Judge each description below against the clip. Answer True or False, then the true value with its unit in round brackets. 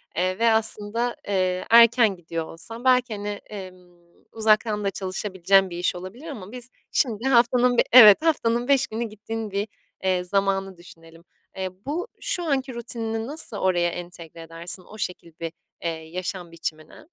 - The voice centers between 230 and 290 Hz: False (205 Hz)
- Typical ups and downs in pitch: True (4.6 semitones)